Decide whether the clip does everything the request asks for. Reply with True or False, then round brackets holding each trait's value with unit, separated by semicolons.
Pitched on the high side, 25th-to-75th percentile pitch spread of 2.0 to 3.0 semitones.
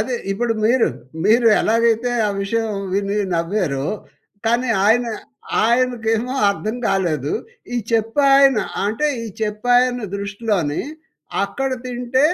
False (225 Hz; 3.5 semitones)